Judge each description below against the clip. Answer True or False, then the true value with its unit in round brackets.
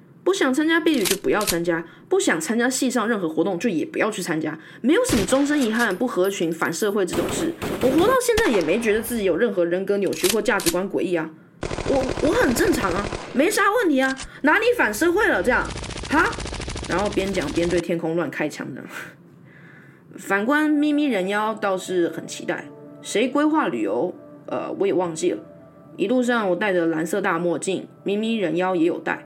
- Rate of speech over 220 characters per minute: True (290 characters per minute)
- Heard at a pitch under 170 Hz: False (210 Hz)